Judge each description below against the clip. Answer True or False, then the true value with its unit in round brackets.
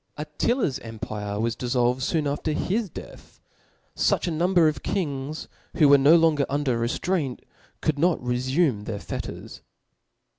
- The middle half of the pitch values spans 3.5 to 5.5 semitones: True (4.8 semitones)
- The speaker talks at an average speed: True (145 wpm)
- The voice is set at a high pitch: False (140 Hz)